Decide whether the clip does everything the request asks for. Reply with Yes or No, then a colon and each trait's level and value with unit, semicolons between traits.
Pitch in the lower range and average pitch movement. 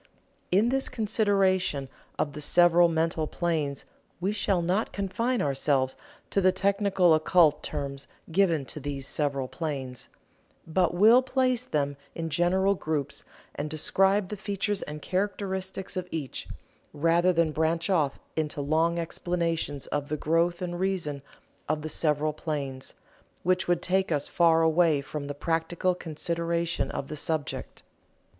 No: medium, 165 Hz; average, 3.9 semitones